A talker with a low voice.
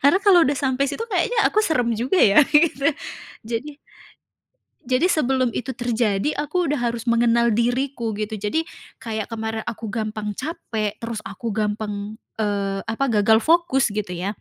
No: high, 235 Hz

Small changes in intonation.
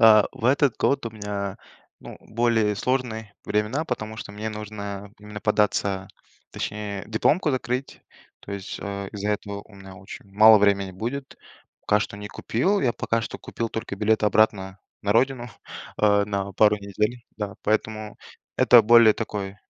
Yes: narrow, 2.0 semitones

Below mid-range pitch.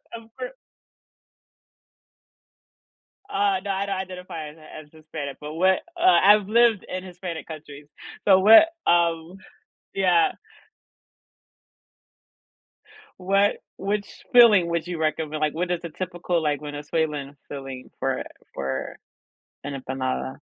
No: medium, 170 Hz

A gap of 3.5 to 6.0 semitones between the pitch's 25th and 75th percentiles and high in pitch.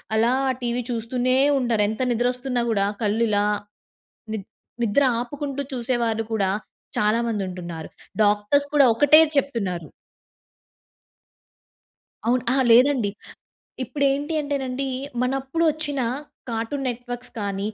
Yes: average, 3.8 semitones; high, 245 Hz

